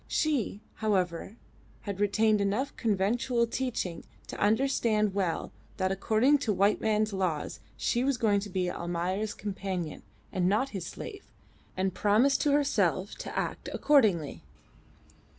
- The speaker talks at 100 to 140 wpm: Yes, slow, 135 wpm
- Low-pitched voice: No, high, 205 Hz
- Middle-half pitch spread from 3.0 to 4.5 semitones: Yes, average, 3.8 semitones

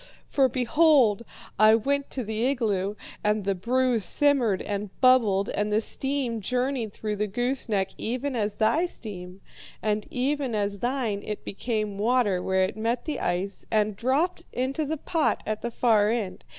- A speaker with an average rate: Yes, average, 165 wpm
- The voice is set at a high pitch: Yes, high, 225 Hz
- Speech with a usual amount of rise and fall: Yes, average, 3.9 semitones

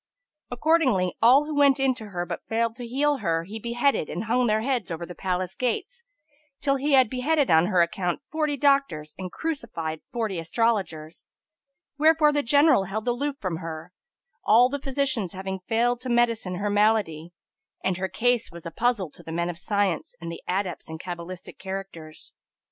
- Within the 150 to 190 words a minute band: Yes, average, 180 wpm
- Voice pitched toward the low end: No, high, 220 Hz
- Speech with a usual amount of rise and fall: No, wide, 6.6 semitones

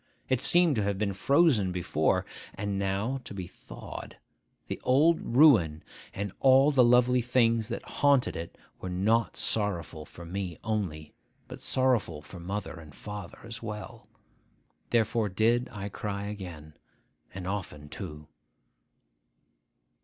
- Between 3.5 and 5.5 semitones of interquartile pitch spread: Yes, average, 4.9 semitones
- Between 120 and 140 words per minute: Yes, slow, 135 wpm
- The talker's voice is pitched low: Yes, low, 105 Hz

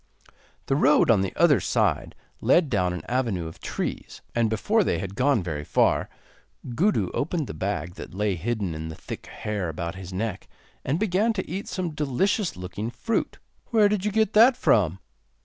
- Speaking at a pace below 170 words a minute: No, average, 185 wpm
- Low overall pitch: Yes, low, 120 Hz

